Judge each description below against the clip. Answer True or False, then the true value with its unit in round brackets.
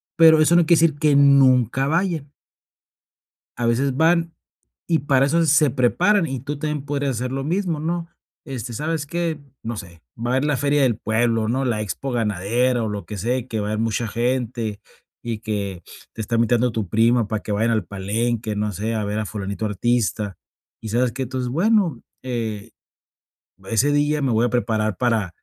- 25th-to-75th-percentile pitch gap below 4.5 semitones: False (4.8 semitones)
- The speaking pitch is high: False (120 Hz)